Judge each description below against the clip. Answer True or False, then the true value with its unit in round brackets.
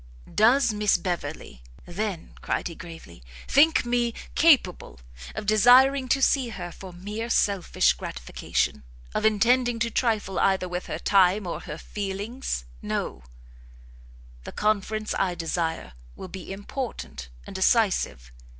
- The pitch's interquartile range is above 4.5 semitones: True (4.9 semitones)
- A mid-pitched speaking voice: False (200 Hz)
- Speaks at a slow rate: True (130 wpm)